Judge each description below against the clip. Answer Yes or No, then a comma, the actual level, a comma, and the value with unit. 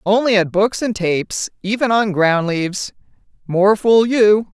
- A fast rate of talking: No, average, 155 wpm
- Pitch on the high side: Yes, high, 205 Hz